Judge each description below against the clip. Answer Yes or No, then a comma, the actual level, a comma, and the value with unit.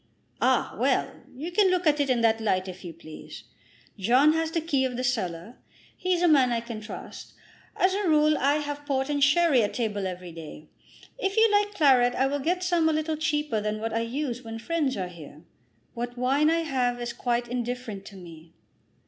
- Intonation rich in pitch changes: Yes, wide, 5.7 semitones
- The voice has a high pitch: Yes, very high, 255 Hz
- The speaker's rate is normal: No, fast, 210 wpm